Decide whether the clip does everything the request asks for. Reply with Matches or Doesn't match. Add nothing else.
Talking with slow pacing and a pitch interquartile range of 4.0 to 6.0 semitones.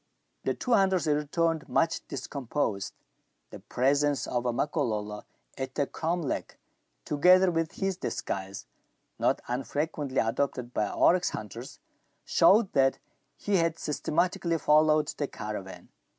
Matches